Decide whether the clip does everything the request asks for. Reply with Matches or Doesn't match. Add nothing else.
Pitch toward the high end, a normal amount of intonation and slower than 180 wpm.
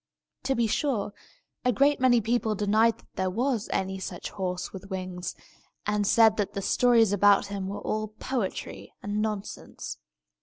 Matches